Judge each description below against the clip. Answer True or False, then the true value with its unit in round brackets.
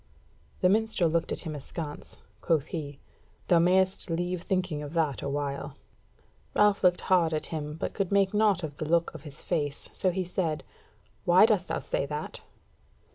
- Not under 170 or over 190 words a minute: True (175 wpm)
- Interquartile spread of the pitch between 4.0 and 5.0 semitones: False (3.5 semitones)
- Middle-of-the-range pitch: True (170 Hz)